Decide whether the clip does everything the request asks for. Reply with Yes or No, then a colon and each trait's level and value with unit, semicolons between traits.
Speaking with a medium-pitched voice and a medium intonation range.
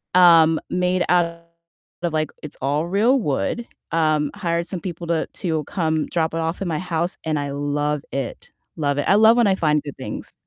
Yes: medium, 165 Hz; average, 3.0 semitones